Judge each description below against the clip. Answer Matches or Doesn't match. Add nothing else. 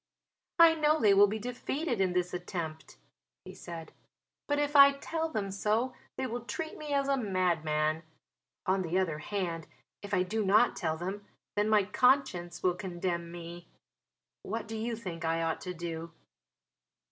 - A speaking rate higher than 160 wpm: Matches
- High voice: Matches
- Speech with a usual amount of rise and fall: Doesn't match